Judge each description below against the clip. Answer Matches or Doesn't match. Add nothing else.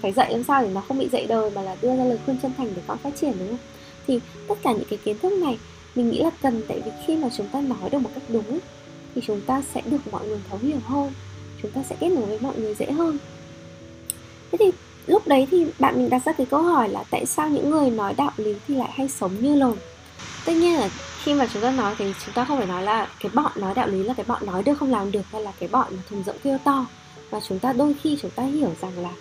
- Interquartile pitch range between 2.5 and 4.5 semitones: Doesn't match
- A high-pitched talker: Matches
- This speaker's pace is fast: Matches